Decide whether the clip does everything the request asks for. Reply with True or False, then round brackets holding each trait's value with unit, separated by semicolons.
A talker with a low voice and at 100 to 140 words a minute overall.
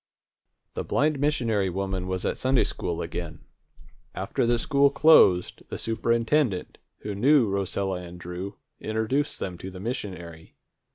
True (100 Hz; 135 wpm)